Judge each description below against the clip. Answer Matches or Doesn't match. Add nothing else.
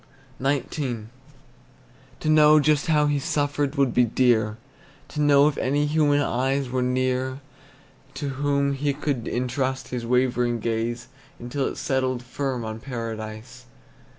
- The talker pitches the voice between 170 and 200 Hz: Doesn't match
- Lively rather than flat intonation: Doesn't match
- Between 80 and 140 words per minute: Matches